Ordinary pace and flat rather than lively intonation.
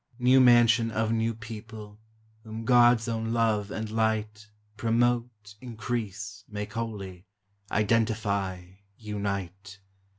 No: slow, 100 wpm; narrow, 1.8 semitones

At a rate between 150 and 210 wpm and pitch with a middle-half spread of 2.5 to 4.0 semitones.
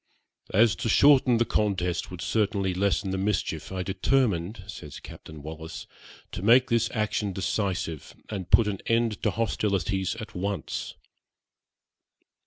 No: slow, 135 wpm; average, 3.3 semitones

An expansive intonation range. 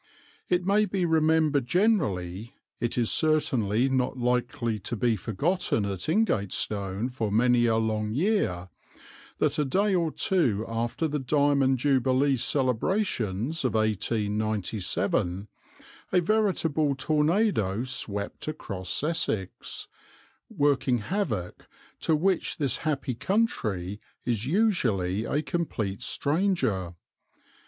Yes: wide, 6.9 semitones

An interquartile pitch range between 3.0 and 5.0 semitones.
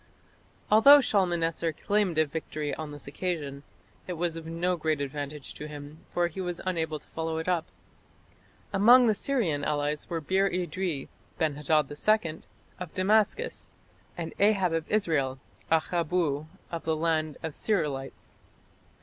Yes: average, 3.4 semitones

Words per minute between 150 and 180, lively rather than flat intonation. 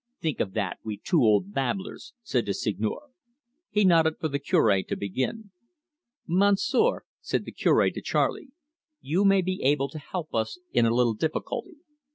Yes: average, 165 wpm; wide, 9.0 semitones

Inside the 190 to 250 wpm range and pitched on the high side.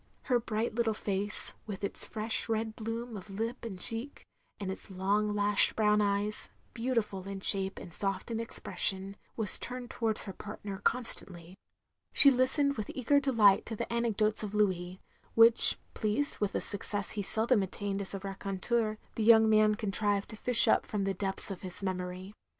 No: average, 180 wpm; high, 210 Hz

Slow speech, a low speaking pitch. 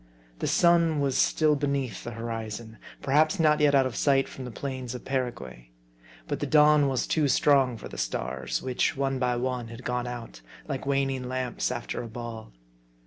No: average, 185 wpm; low, 130 Hz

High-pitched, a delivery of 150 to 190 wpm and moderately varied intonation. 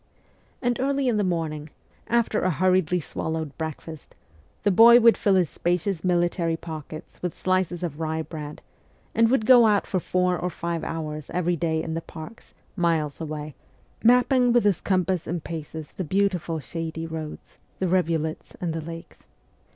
No: medium, 170 Hz; average, 165 wpm; average, 3.2 semitones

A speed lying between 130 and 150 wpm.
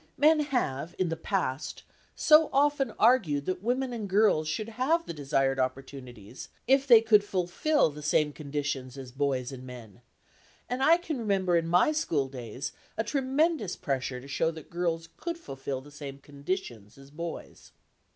No: average, 160 wpm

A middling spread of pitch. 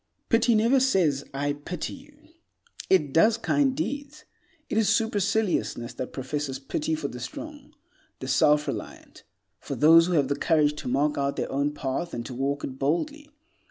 No: wide, 8.3 semitones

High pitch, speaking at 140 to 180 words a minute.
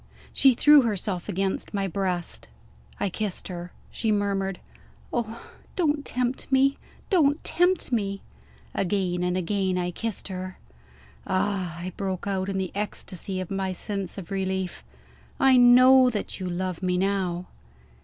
Yes: high, 195 Hz; average, 145 wpm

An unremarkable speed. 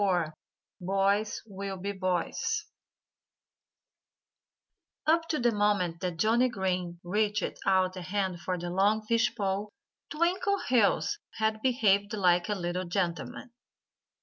No: slow, 120 wpm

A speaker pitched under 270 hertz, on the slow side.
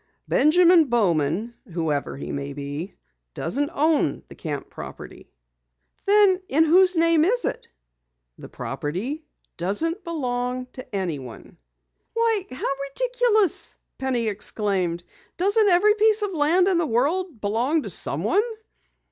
No: very high, 290 Hz; slow, 120 wpm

